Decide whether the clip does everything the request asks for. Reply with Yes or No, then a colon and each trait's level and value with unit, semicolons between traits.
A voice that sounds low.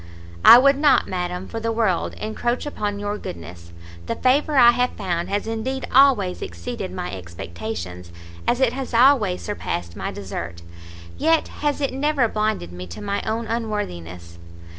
No: high, 210 Hz